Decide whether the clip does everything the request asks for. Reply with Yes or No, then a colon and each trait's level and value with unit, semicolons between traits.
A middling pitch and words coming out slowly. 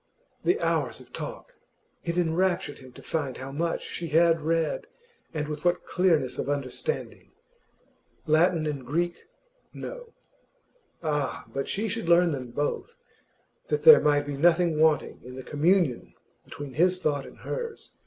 No: medium, 160 Hz; average, 150 wpm